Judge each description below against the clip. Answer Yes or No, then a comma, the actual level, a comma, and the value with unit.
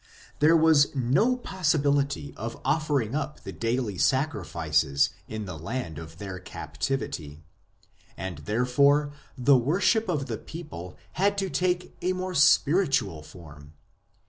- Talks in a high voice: No, low, 135 Hz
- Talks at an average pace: No, slow, 130 wpm